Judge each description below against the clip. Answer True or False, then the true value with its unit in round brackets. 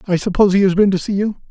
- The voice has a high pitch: True (195 Hz)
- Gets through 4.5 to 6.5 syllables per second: False (7.7 syllables/s)